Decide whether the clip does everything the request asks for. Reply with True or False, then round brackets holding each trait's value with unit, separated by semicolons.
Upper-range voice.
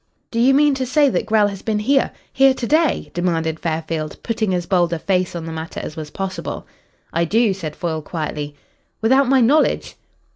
True (195 Hz)